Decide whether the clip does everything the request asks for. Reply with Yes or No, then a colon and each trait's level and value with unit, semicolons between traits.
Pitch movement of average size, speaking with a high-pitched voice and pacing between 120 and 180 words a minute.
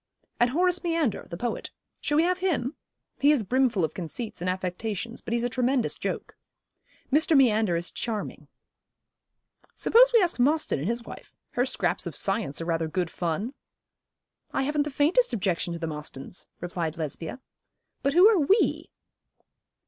No: wide, 8.9 semitones; high, 240 Hz; average, 165 wpm